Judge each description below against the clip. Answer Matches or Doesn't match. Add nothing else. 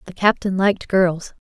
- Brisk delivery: Doesn't match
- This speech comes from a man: Doesn't match